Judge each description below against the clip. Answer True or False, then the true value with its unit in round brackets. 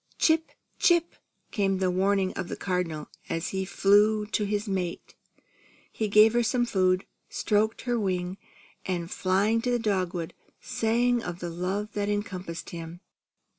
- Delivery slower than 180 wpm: True (150 wpm)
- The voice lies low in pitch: False (200 Hz)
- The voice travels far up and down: False (3.2 semitones)